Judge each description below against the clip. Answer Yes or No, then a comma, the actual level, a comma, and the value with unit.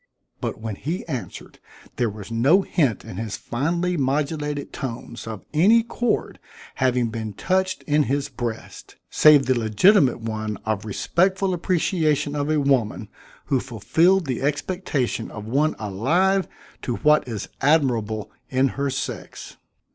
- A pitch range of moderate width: No, wide, 6.0 semitones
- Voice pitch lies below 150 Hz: Yes, low, 135 Hz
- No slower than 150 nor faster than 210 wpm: No, average, 140 wpm